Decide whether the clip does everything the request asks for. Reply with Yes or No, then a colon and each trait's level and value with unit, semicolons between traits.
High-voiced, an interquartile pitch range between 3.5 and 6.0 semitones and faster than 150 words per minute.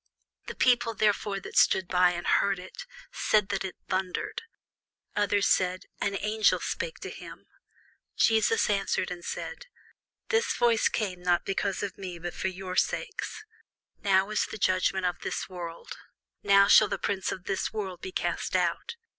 No: high, 195 Hz; narrow, 2.4 semitones; average, 165 wpm